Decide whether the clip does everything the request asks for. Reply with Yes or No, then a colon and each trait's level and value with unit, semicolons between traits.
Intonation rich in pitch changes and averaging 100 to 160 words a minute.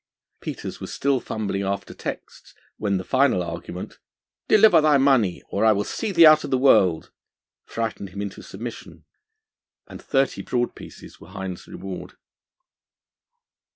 Yes: wide, 6.0 semitones; average, 145 wpm